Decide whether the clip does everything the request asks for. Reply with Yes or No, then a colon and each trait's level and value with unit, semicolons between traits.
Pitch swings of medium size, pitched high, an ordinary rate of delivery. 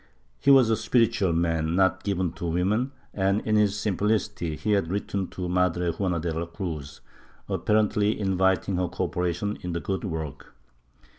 No: average, 3.4 semitones; very low, 95 Hz; average, 160 wpm